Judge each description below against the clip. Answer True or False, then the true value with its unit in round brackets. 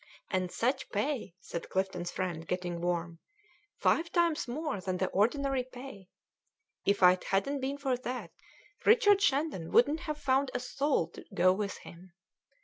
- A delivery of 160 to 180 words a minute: False (150 wpm)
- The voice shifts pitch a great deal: True (7.4 semitones)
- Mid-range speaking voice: False (235 Hz)